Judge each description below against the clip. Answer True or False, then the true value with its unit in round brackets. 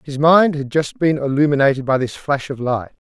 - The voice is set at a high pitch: False (140 Hz)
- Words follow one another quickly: True (215 wpm)